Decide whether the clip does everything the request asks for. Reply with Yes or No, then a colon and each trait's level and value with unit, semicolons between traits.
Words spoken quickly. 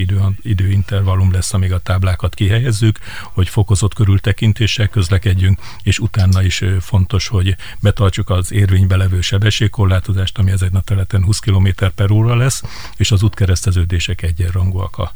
No: average, 140 wpm